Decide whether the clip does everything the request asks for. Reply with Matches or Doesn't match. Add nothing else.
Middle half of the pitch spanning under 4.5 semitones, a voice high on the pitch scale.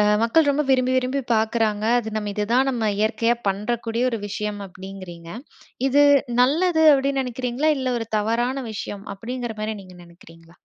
Matches